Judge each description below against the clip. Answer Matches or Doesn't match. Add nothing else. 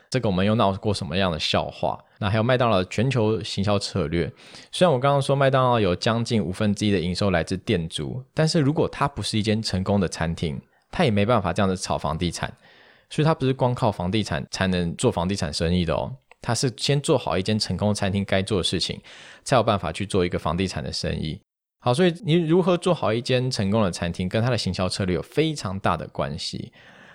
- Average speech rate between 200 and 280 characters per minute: Doesn't match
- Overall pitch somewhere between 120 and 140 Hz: Doesn't match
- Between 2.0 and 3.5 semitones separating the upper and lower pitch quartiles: Doesn't match